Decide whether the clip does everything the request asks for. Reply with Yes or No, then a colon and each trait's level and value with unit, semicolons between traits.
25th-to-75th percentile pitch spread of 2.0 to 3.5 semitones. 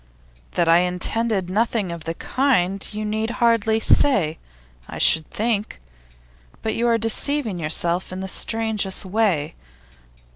No: average, 4.1 semitones